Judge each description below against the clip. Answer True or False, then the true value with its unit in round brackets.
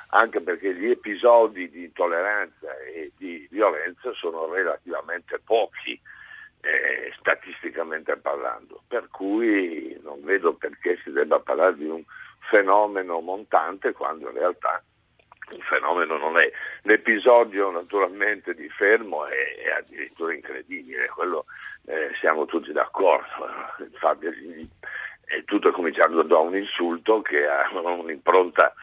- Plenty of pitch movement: True (7.5 semitones)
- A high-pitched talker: True (395 Hz)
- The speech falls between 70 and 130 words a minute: True (120 wpm)